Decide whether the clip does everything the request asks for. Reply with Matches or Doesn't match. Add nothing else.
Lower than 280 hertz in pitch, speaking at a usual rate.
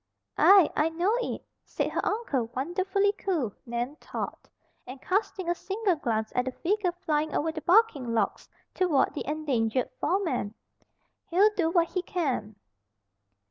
Doesn't match